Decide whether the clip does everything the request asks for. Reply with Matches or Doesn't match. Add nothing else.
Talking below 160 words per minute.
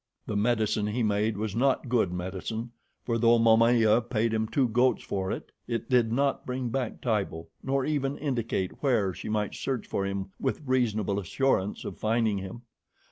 Doesn't match